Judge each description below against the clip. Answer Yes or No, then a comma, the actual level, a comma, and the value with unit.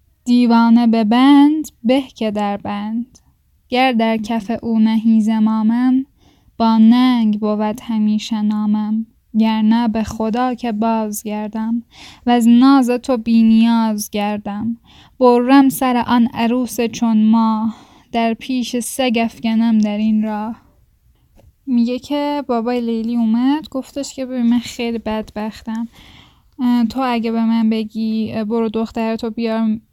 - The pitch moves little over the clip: Yes, narrow, 1.8 semitones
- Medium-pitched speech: No, high, 230 Hz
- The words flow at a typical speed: Yes, average, 130 wpm